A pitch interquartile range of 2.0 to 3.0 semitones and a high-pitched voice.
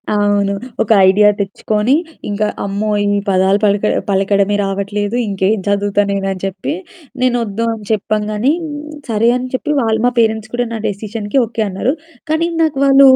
Yes: narrow, 2.4 semitones; high, 210 Hz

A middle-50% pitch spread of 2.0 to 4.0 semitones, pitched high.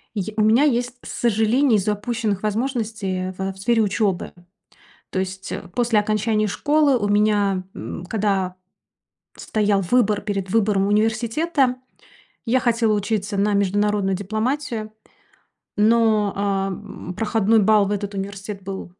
Yes: narrow, 2.4 semitones; high, 210 Hz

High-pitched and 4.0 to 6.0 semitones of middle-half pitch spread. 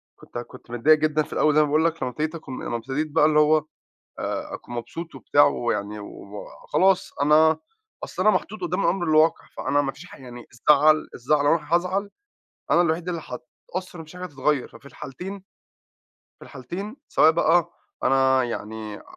No: medium, 150 Hz; average, 4.4 semitones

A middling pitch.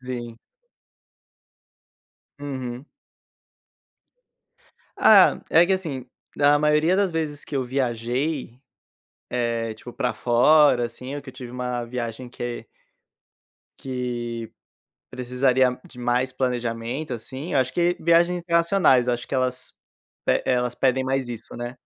No: low, 130 Hz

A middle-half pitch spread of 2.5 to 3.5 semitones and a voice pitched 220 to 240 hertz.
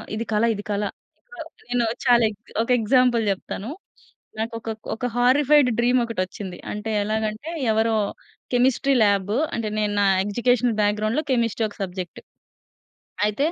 Yes: average, 2.8 semitones; high, 225 Hz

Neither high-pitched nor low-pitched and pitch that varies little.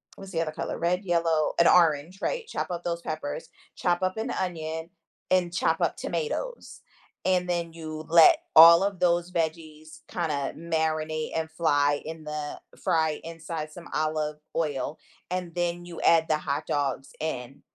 Yes: medium, 165 Hz; narrow, 2.0 semitones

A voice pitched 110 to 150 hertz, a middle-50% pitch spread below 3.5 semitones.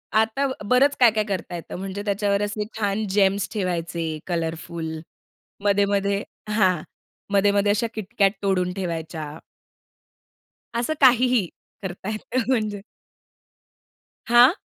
No: high, 200 Hz; average, 3.0 semitones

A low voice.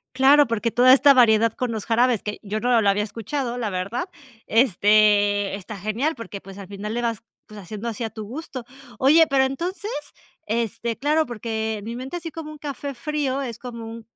No: high, 230 Hz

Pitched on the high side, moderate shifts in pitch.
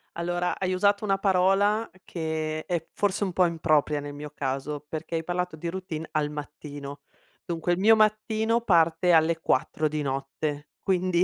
No: medium, 170 Hz; average, 3.7 semitones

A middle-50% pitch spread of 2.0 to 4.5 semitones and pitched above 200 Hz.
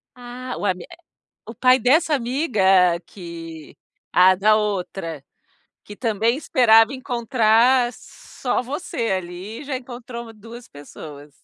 No: average, 5.0 semitones; high, 230 Hz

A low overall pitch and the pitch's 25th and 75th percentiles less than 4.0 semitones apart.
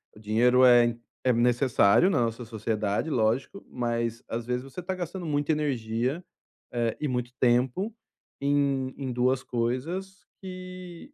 No: low, 125 Hz; average, 4.7 semitones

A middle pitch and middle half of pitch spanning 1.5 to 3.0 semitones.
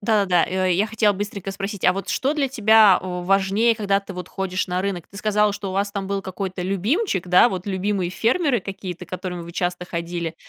No: high, 195 Hz; narrow, 2.4 semitones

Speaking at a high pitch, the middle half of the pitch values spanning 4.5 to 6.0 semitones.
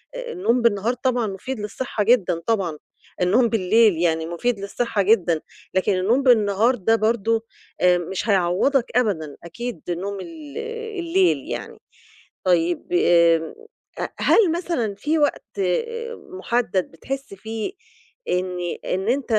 Yes: high, 215 Hz; average, 5.3 semitones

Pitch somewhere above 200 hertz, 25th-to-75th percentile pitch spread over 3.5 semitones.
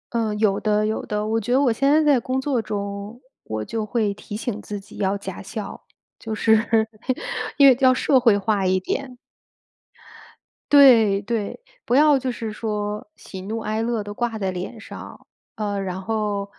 No: high, 220 Hz; average, 2.9 semitones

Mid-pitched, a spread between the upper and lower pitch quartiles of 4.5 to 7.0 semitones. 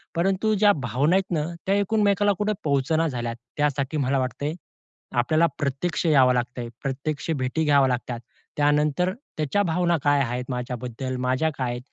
Yes: medium, 145 Hz; average, 4.8 semitones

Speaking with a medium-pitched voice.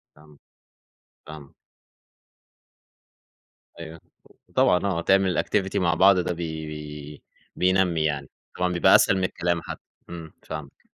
No: very low, 85 Hz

